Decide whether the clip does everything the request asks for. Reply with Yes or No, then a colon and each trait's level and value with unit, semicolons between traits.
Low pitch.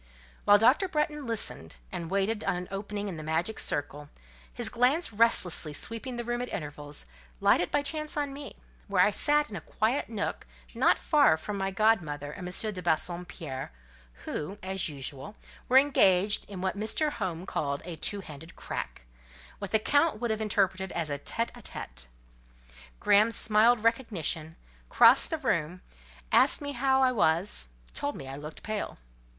No: high, 200 Hz